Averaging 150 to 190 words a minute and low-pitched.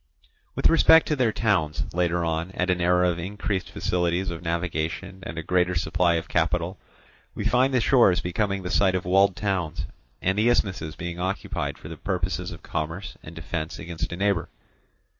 Yes: average, 180 wpm; very low, 90 Hz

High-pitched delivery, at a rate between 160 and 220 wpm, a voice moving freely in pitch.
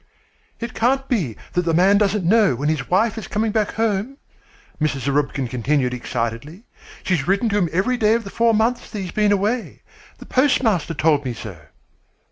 Yes: high, 195 Hz; average, 185 wpm; wide, 7.3 semitones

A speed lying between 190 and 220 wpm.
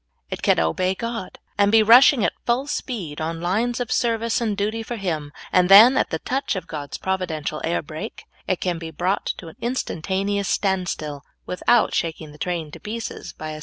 Yes: average, 200 wpm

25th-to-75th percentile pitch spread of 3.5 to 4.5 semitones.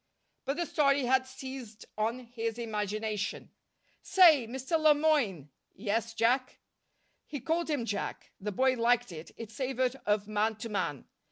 Yes: average, 4.0 semitones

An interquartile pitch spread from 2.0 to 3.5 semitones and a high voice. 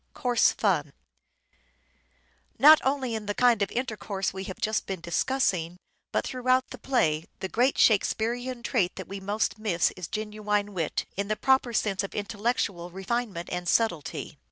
No: average, 4.3 semitones; high, 210 Hz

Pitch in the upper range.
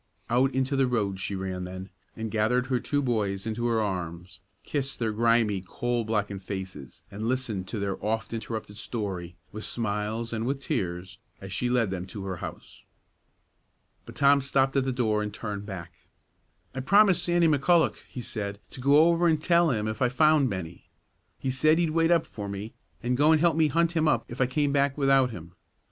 No: low, 115 Hz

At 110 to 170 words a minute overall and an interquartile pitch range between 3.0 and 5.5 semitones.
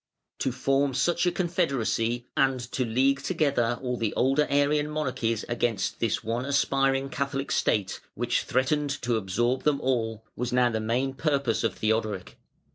Yes: average, 155 wpm; average, 3.3 semitones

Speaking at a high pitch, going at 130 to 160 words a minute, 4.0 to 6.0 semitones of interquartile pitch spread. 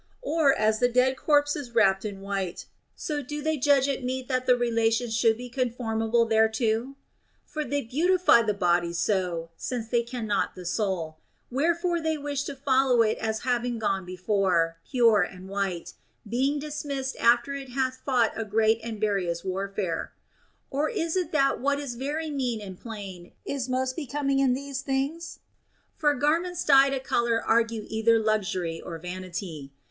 No: high, 240 Hz; average, 170 wpm; average, 5.1 semitones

